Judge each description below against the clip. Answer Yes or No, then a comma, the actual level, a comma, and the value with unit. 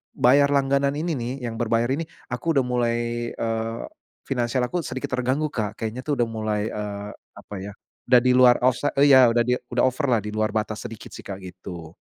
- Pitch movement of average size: Yes, average, 3.3 semitones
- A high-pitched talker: No, low, 120 Hz